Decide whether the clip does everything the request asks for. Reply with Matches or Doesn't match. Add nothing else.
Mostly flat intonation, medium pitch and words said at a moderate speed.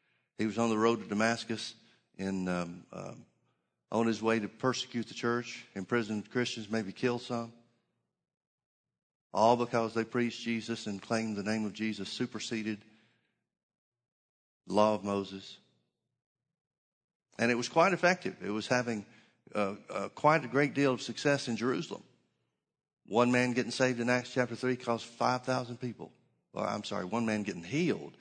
Doesn't match